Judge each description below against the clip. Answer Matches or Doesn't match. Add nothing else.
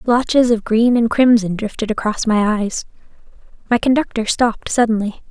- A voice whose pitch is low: Doesn't match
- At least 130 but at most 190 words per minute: Matches